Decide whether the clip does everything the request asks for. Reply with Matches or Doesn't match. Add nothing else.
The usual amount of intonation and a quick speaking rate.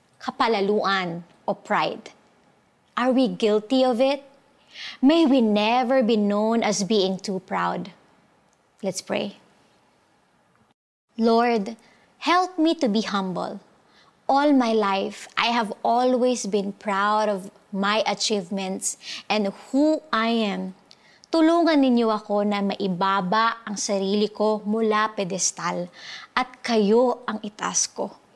Doesn't match